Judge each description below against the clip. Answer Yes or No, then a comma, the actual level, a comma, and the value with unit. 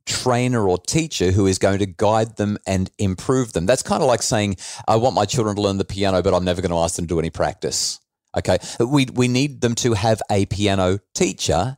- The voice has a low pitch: Yes, low, 105 Hz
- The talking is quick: Yes, fast, 235 wpm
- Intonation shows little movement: No, average, 4.2 semitones